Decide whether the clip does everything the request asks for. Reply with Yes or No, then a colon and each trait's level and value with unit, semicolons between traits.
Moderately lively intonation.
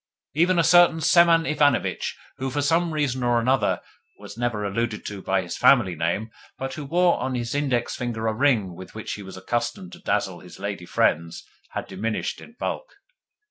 No: wide, 6.9 semitones